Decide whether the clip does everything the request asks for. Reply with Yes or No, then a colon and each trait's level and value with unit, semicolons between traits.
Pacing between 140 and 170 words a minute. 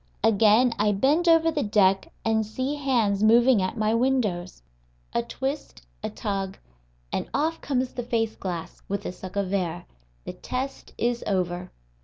Yes: average, 160 wpm